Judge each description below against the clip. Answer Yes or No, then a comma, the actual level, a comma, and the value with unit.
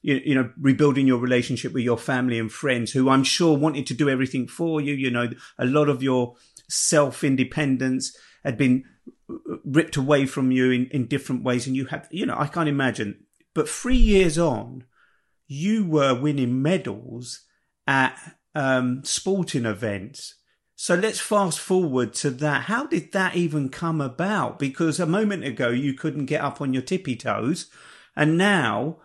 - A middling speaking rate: Yes, average, 170 wpm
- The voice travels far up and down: No, average, 3.9 semitones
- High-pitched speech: No, medium, 140 Hz